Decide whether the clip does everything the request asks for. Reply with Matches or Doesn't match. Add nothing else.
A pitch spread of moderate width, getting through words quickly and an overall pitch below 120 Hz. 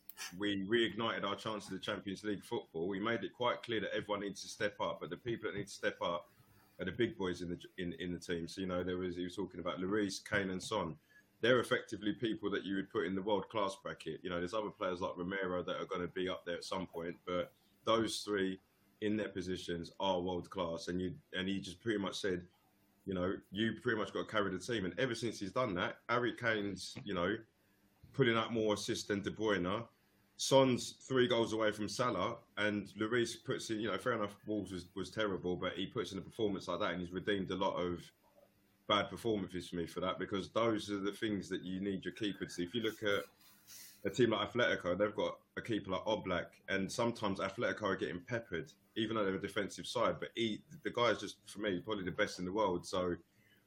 Matches